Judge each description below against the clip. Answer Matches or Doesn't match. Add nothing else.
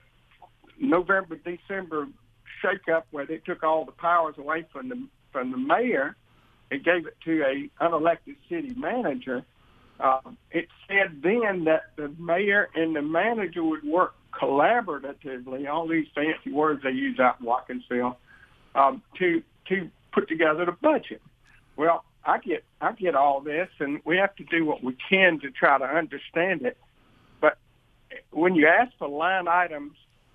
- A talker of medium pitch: Matches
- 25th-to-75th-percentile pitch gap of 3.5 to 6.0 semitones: Matches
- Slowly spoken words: Doesn't match